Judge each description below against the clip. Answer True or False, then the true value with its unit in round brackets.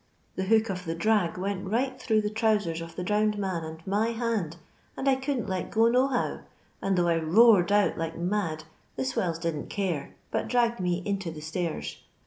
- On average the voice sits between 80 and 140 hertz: False (190 Hz)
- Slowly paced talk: False (200 wpm)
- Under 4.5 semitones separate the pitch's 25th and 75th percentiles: False (4.8 semitones)